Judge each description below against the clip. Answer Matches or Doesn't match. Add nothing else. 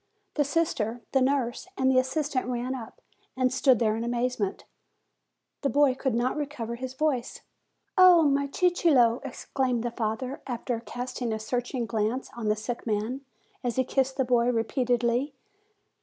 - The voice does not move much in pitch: Matches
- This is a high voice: Matches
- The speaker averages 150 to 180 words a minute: Matches